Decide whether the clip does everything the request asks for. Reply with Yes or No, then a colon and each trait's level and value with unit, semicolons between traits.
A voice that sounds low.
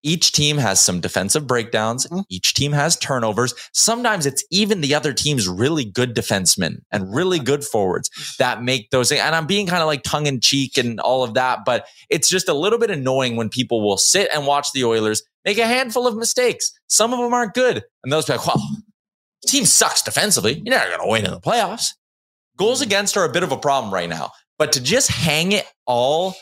No: medium, 145 Hz